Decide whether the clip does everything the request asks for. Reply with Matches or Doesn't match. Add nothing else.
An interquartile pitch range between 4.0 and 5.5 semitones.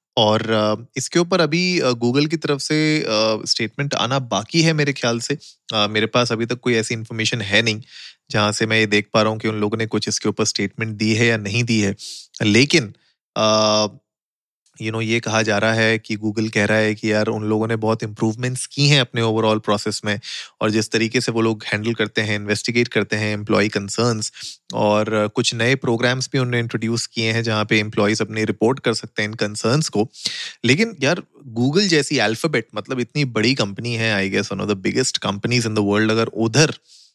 Doesn't match